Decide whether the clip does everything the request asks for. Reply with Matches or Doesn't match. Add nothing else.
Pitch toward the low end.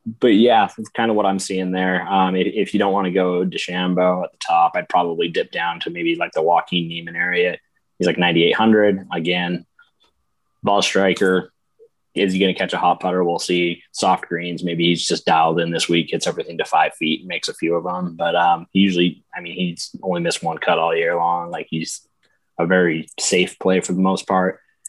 Matches